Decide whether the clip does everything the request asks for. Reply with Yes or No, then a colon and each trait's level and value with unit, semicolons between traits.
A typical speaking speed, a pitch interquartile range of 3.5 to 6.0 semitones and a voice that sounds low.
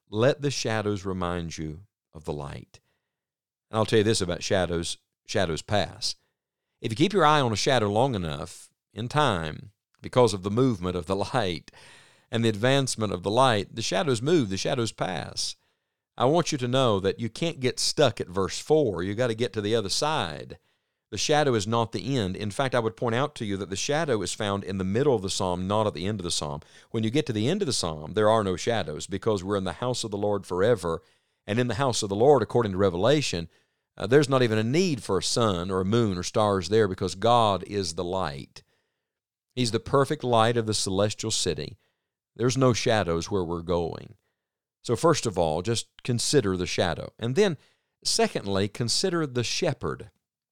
No: fast, 215 wpm; average, 4.6 semitones; low, 110 Hz